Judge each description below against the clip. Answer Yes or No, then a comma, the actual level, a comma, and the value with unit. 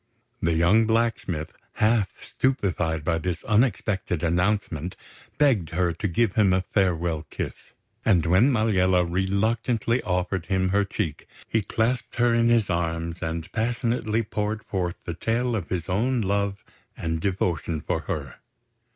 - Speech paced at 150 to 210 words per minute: No, average, 140 wpm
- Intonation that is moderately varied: Yes, average, 4.7 semitones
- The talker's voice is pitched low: Yes, very low, 95 Hz